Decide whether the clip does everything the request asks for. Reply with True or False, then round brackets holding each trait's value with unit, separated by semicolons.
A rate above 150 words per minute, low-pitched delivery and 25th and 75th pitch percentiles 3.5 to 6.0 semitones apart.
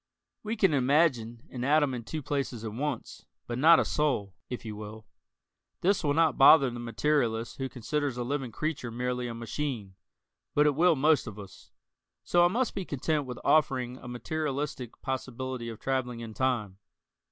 True (175 wpm; 130 Hz; 4.1 semitones)